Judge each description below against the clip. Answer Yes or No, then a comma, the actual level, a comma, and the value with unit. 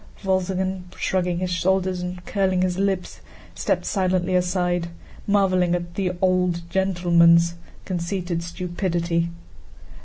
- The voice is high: No, medium, 180 Hz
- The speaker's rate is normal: No, slow, 110 wpm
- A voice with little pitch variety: Yes, narrow, 1.4 semitones